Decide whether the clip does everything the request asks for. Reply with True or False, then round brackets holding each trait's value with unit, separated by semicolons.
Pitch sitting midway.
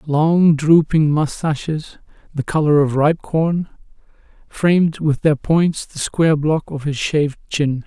True (155 Hz)